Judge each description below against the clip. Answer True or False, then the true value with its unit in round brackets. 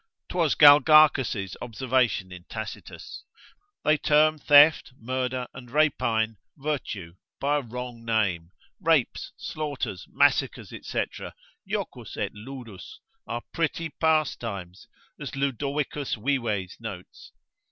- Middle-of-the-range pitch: False (130 Hz)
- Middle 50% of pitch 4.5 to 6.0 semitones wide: True (5.0 semitones)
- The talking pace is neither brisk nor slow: False (100 wpm)